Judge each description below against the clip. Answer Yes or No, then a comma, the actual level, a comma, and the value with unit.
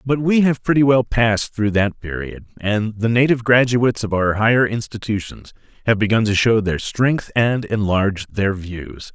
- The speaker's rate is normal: Yes, average, 175 wpm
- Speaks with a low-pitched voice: Yes, low, 110 Hz